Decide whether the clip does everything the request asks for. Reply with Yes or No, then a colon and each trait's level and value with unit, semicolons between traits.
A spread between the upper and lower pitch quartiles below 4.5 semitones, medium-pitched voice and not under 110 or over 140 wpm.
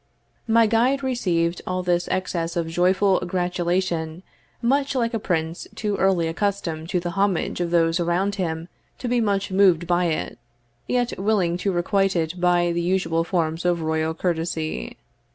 No: average, 2.9 semitones; medium, 180 Hz; average, 160 wpm